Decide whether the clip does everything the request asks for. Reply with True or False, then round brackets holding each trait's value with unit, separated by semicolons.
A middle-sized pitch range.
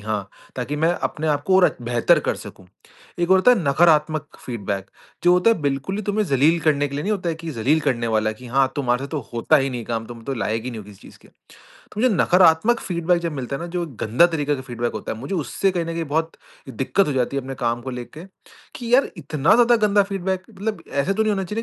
False (6.5 semitones)